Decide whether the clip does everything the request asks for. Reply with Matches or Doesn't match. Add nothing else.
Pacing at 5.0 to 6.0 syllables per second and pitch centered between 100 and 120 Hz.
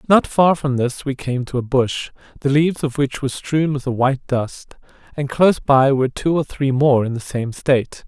Doesn't match